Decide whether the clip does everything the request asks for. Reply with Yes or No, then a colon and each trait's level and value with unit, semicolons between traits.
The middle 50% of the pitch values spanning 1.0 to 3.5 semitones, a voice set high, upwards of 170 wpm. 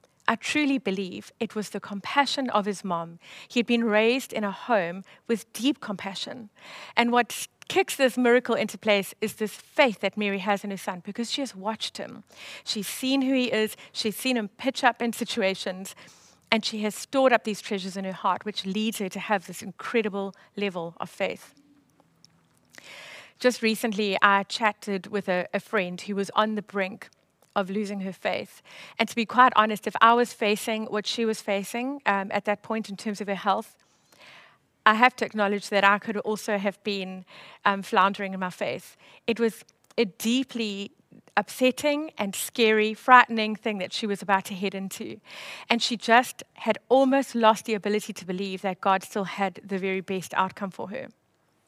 Yes: average, 2.8 semitones; high, 210 Hz; average, 190 wpm